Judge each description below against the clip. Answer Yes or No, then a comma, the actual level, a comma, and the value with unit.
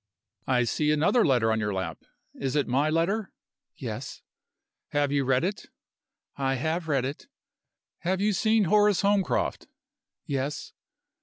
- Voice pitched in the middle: Yes, medium, 150 Hz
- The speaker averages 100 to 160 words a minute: Yes, average, 140 wpm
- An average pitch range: No, wide, 6.2 semitones